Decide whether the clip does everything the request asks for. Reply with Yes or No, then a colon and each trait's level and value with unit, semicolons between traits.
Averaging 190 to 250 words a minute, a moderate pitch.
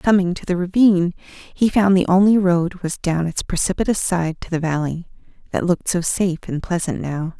Yes: average, 195 wpm; medium, 180 Hz